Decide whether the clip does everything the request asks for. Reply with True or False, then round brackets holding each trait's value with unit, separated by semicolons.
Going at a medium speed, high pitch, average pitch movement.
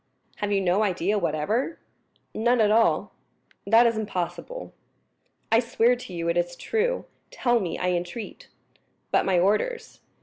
True (145 wpm; 210 Hz; 4.9 semitones)